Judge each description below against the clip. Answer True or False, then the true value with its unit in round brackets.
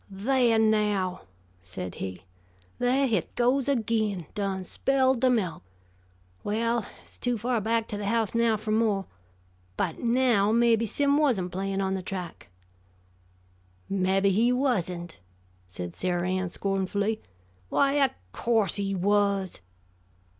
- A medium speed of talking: False (130 wpm)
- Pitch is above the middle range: True (210 Hz)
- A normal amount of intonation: True (3.8 semitones)